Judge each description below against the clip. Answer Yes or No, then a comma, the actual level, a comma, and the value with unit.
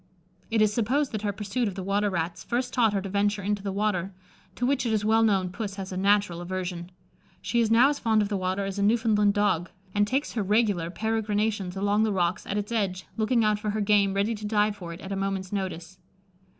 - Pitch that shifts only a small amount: Yes, narrow, 2.2 semitones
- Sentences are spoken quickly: Yes, fast, 240 wpm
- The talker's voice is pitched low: No, high, 205 Hz